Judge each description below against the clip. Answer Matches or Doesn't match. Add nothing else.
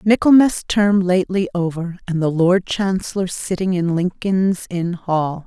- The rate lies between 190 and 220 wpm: Doesn't match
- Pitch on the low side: Doesn't match